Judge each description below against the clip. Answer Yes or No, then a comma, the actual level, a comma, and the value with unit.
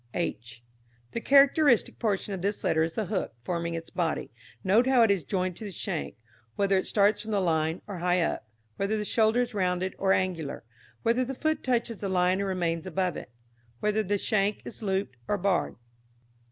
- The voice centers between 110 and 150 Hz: No, high, 195 Hz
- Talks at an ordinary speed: Yes, average, 195 wpm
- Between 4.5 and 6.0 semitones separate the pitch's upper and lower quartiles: No, average, 3.4 semitones